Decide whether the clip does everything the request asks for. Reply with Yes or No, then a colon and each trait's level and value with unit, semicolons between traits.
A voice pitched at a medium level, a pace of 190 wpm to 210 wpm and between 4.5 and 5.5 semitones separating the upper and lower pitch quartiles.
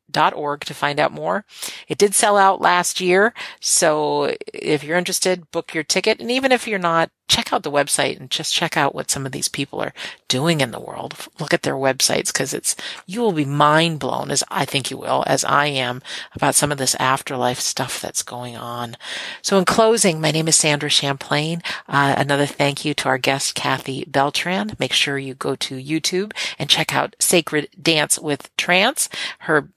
Yes: medium, 150 Hz; fast, 205 wpm; average, 4.9 semitones